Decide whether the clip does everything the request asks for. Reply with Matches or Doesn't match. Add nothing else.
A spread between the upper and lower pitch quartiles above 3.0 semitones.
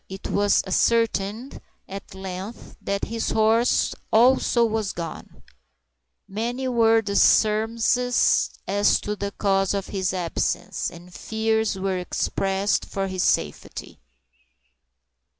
Doesn't match